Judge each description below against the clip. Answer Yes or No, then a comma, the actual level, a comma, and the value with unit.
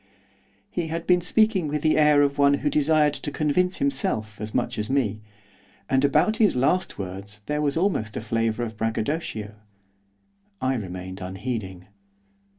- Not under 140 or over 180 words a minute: Yes, average, 155 wpm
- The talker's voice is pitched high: No, medium, 140 Hz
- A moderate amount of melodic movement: No, wide, 6.4 semitones